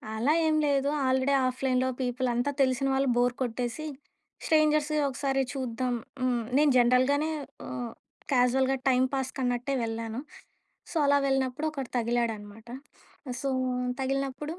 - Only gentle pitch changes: Yes, narrow, 2.1 semitones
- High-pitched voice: Yes, very high, 260 Hz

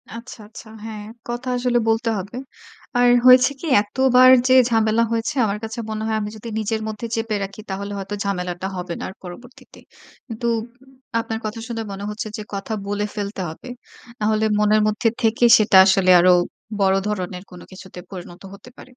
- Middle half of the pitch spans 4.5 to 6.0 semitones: No, average, 2.8 semitones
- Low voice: No, high, 215 Hz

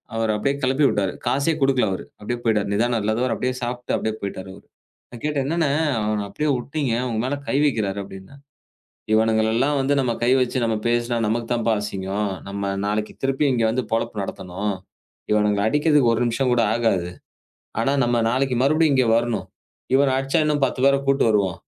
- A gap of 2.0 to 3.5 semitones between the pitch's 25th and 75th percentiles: No, average, 4.1 semitones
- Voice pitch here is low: Yes, low, 120 Hz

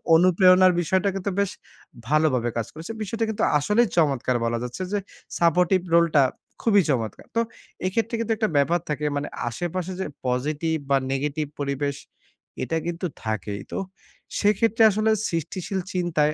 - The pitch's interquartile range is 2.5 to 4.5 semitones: No, average, 5.0 semitones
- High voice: No, medium, 170 Hz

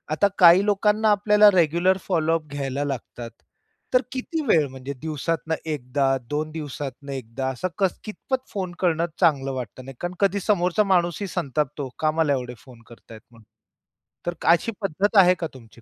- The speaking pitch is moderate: Yes, medium, 160 Hz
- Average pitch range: No, wide, 5.8 semitones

